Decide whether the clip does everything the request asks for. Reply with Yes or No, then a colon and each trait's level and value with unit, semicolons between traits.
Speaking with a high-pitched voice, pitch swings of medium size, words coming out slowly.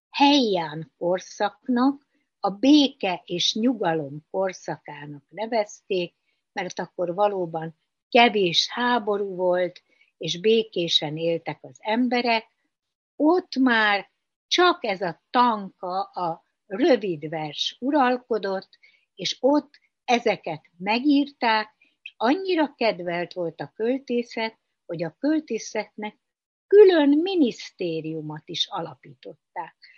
No: high, 210 Hz; wide, 6.6 semitones; slow, 90 wpm